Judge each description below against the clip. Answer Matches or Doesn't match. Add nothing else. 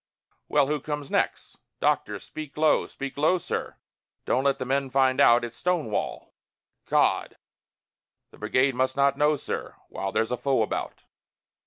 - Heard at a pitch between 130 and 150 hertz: Matches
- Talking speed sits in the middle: Matches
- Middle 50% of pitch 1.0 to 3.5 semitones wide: Matches